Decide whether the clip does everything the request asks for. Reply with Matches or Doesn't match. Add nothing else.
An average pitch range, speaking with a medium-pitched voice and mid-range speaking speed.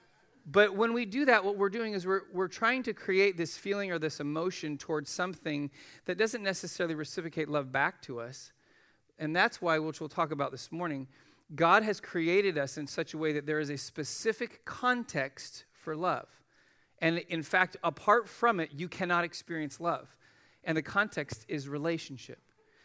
Matches